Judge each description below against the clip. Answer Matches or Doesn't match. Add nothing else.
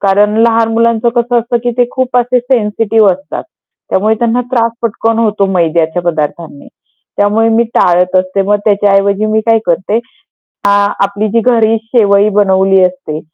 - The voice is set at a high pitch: Matches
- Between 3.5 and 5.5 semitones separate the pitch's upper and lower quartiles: Doesn't match